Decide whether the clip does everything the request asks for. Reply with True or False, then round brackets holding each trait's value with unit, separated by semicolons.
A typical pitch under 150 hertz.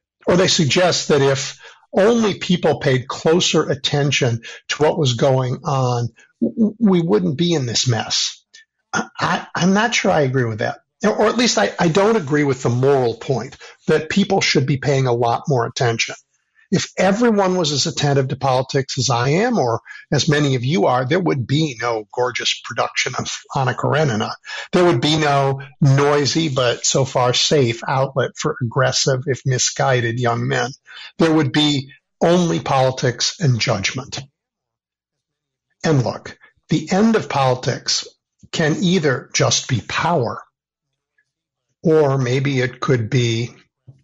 True (140 Hz)